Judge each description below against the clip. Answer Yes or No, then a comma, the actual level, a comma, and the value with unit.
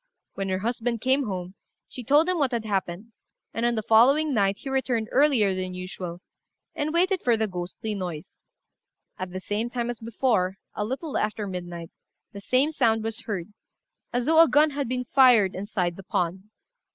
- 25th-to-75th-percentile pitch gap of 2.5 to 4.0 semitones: No, wide, 5.4 semitones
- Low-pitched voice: No, high, 225 Hz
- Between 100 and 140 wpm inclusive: No, average, 185 wpm